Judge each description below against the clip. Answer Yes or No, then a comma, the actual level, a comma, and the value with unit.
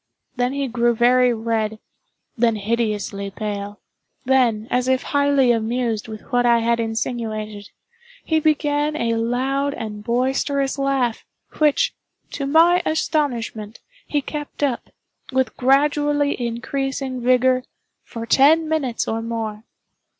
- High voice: Yes, high, 245 Hz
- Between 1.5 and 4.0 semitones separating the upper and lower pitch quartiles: Yes, average, 3.5 semitones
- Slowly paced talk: Yes, slow, 115 wpm